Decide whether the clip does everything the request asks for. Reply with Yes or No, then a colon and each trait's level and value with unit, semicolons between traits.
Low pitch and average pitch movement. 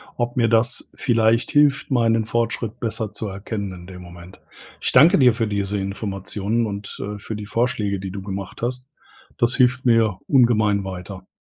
Yes: low, 110 Hz; average, 3.3 semitones